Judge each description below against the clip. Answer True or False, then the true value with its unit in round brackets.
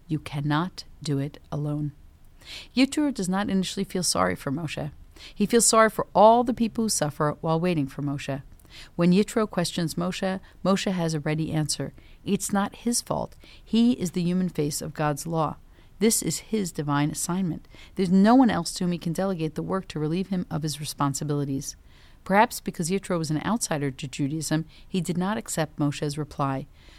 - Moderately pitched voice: True (165 Hz)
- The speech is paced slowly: False (185 wpm)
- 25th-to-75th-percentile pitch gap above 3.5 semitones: True (4.7 semitones)